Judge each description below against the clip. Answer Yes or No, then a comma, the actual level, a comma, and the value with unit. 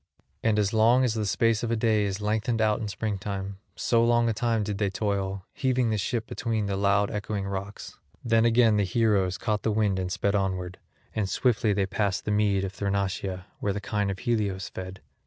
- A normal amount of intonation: No, narrow, 2.3 semitones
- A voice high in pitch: No, low, 105 Hz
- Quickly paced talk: Yes, fast, 210 wpm